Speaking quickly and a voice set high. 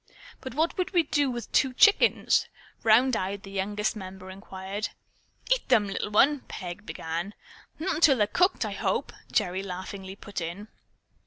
No: average, 160 wpm; high, 205 Hz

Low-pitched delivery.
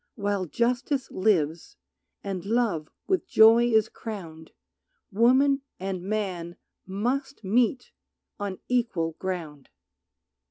No: high, 205 Hz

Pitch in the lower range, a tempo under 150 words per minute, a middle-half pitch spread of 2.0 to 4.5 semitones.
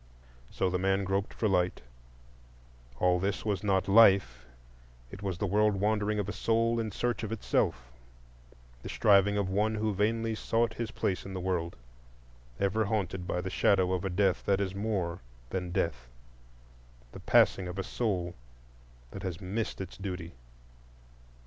No: very low, 95 Hz; average, 155 wpm; average, 2.9 semitones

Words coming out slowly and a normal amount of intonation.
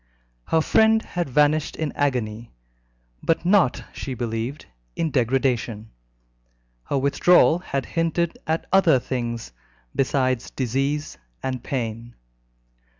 Yes: slow, 105 wpm; average, 5.0 semitones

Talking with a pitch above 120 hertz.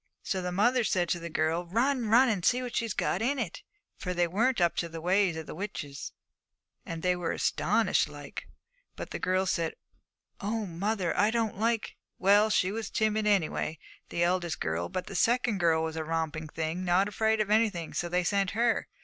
Yes: medium, 185 Hz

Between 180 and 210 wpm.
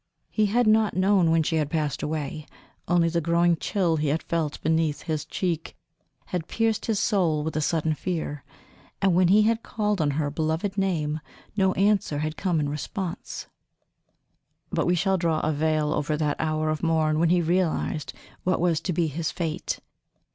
Yes: average, 185 wpm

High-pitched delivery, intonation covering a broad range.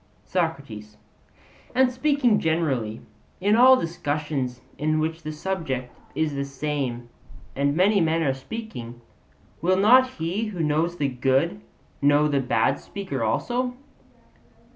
No: medium, 155 Hz; wide, 6.1 semitones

